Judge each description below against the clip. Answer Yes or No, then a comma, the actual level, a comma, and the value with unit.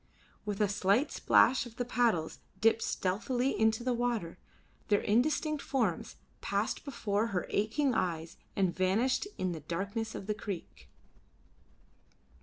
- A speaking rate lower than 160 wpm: Yes, slow, 135 wpm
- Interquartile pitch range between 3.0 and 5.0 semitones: Yes, average, 4.5 semitones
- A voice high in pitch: Yes, high, 215 Hz